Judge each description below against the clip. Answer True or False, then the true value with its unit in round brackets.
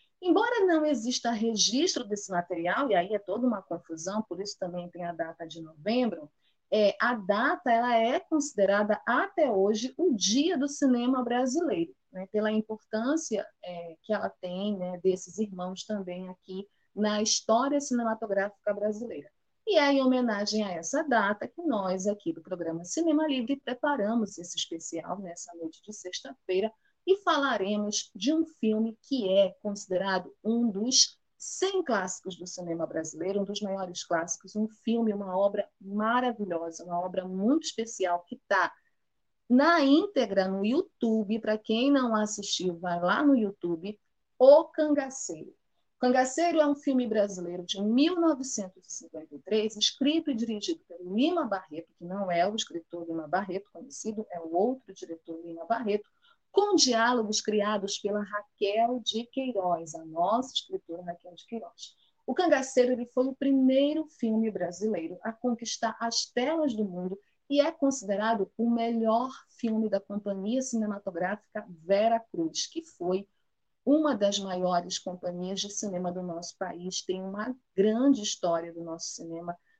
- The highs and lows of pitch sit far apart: True (5.7 semitones)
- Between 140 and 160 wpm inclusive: True (150 wpm)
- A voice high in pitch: True (215 Hz)